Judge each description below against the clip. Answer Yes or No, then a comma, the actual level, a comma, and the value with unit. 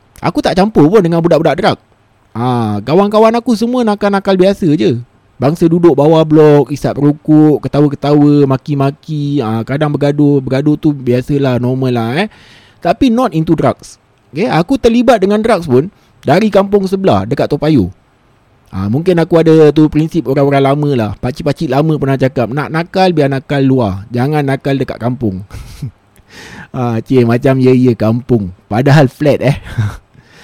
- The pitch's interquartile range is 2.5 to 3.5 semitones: No, average, 4.7 semitones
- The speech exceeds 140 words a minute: Yes, fast, 155 wpm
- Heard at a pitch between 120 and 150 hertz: Yes, medium, 140 Hz